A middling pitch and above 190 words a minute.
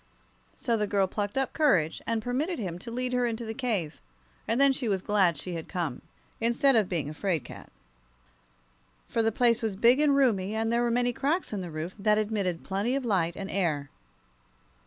No: high, 220 Hz; fast, 205 wpm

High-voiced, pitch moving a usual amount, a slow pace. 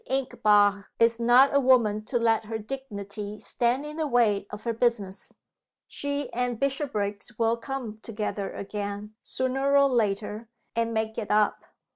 No: high, 230 Hz; average, 3.6 semitones; average, 150 wpm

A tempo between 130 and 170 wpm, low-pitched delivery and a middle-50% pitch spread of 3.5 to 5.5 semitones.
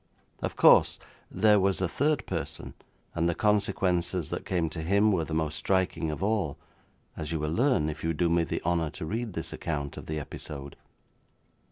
No: average, 190 wpm; very low, 85 Hz; average, 4.0 semitones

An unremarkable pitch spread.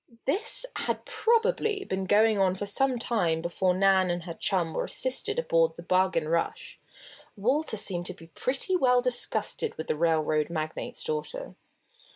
No: wide, 7.9 semitones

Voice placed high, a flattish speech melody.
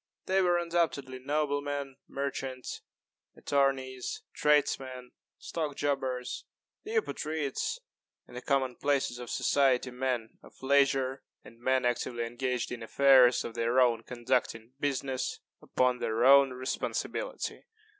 No: low, 130 Hz; narrow, 2.3 semitones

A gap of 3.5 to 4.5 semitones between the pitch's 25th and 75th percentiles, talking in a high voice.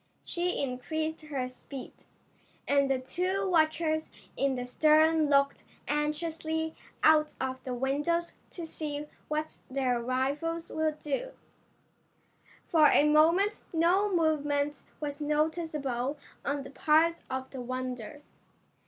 No: average, 2.9 semitones; very high, 300 Hz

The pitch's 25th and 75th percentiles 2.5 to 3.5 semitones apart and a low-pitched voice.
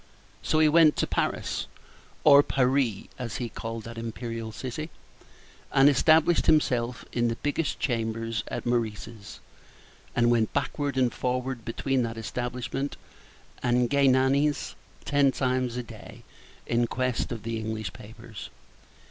Yes: average, 2.9 semitones; low, 125 Hz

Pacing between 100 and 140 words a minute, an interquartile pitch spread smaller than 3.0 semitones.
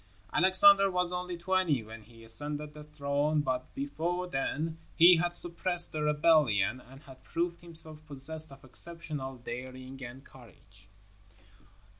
No: slow, 135 wpm; average, 4.7 semitones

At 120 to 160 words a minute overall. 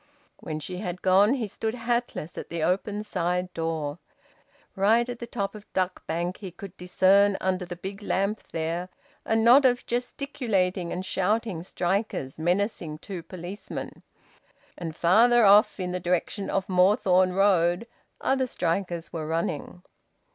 Yes: average, 145 wpm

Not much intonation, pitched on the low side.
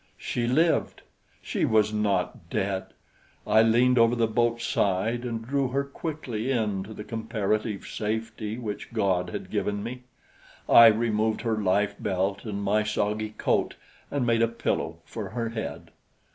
Yes: narrow, 2.1 semitones; low, 110 Hz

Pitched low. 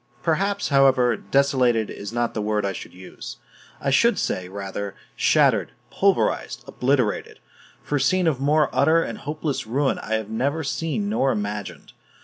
Yes: low, 130 Hz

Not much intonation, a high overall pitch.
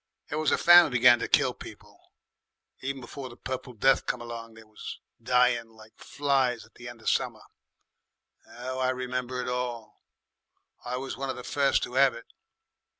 No: narrow, 1.8 semitones; low, 125 Hz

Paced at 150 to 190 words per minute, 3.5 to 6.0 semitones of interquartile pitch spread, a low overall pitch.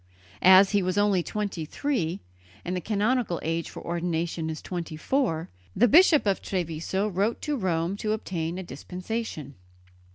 No: average, 155 wpm; average, 4.1 semitones; medium, 185 Hz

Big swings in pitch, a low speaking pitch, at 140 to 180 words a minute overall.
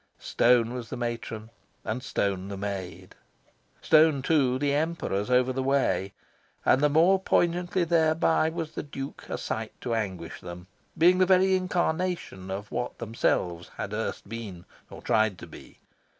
Yes: wide, 7.8 semitones; low, 125 Hz; average, 155 wpm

